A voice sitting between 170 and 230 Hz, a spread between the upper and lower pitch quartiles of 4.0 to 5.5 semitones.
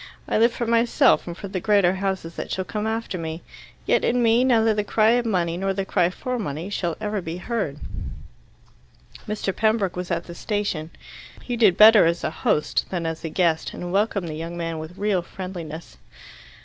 Yes: high, 190 Hz; average, 4.3 semitones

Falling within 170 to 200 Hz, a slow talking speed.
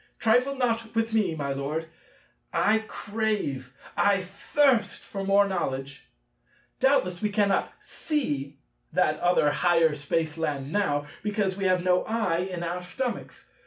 Yes: medium, 185 Hz; slow, 130 wpm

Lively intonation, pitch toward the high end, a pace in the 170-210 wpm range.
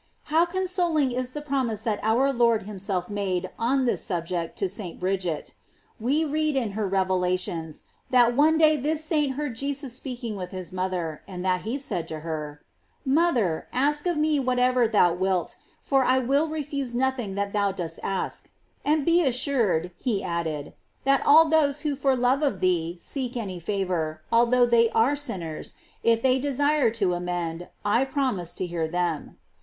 Yes: wide, 7.2 semitones; high, 230 Hz; average, 175 wpm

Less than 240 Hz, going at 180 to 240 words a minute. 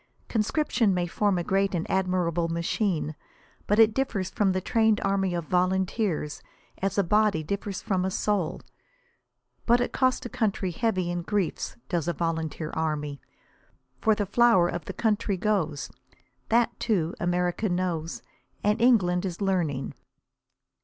No: high, 190 Hz; average, 145 wpm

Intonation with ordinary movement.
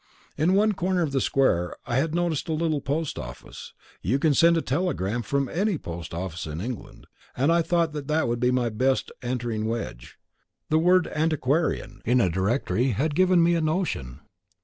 No: wide, 6.0 semitones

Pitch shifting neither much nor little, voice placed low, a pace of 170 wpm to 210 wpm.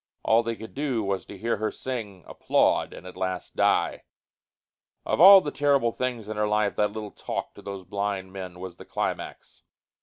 Yes: average, 3.3 semitones; low, 105 Hz; average, 190 wpm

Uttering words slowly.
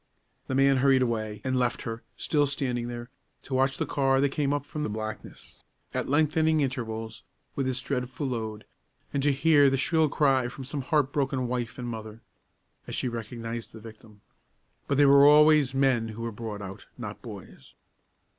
No: average, 185 wpm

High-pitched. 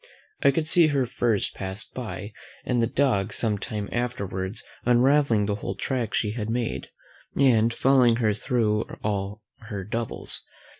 No: low, 115 Hz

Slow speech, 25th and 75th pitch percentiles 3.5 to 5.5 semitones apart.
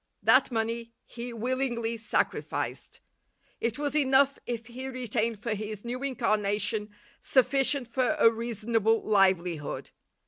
No: slow, 115 wpm; average, 3.0 semitones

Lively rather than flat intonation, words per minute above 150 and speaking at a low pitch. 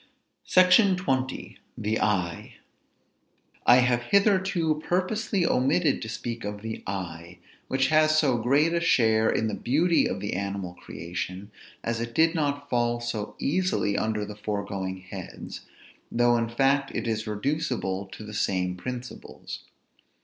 No: wide, 6.8 semitones; average, 140 wpm; low, 120 Hz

